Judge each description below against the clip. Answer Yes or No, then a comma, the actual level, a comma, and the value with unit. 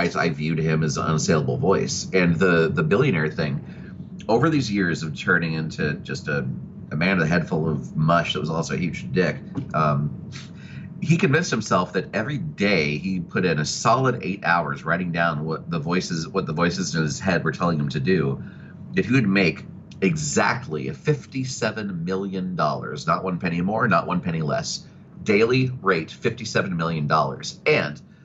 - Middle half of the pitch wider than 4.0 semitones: Yes, average, 4.5 semitones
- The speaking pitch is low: Yes, very low, 85 Hz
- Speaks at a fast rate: No, average, 185 wpm